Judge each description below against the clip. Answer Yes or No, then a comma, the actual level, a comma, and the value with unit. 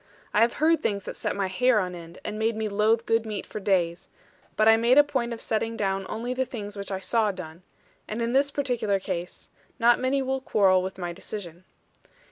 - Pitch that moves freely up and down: No, average, 3.7 semitones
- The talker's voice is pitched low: No, high, 215 Hz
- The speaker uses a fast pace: Yes, fast, 220 wpm